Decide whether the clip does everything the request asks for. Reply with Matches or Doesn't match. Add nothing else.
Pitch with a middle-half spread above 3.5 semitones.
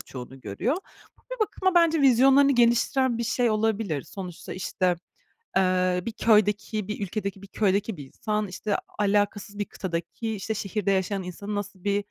Doesn't match